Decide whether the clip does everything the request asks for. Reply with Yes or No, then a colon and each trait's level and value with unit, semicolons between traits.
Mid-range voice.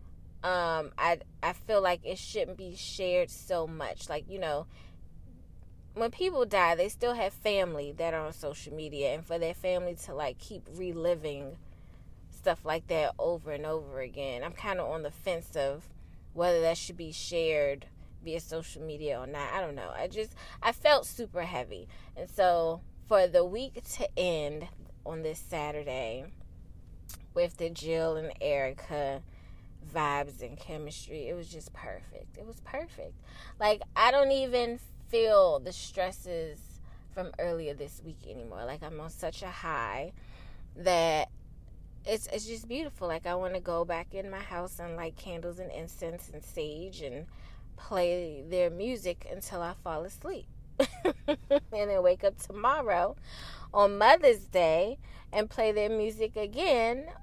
Yes: medium, 170 Hz